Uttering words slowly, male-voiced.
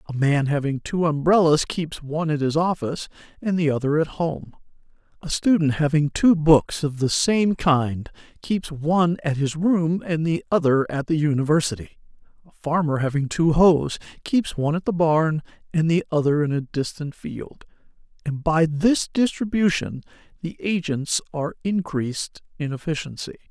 No: average, 160 wpm; male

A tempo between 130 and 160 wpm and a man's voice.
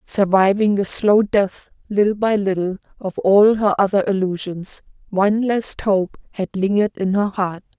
No: average, 155 wpm; female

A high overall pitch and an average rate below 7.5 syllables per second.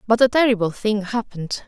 Yes: high, 215 Hz; 5.9 syllables/s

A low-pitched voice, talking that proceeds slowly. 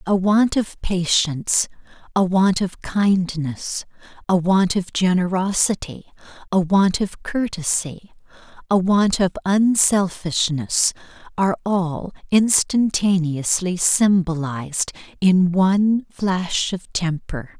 No: medium, 185 Hz; slow, 100 wpm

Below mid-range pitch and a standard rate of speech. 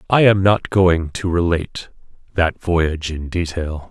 Yes: very low, 85 Hz; average, 155 wpm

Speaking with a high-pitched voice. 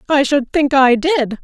Yes: very high, 270 Hz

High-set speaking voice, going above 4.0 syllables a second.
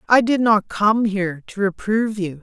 Yes: high, 205 Hz; 5.0 syllables/s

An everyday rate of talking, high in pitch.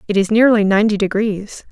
Yes: average, 175 wpm; high, 210 Hz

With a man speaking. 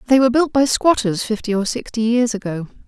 No: female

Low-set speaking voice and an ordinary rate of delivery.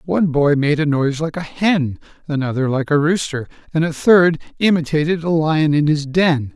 No: medium, 155 Hz; average, 190 wpm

